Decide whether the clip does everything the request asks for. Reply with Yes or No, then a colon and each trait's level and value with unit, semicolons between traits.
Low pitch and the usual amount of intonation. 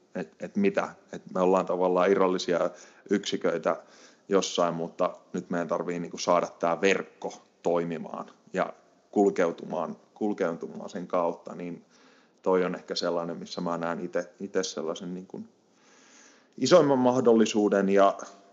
No: very low, 95 Hz; narrow, 2.3 semitones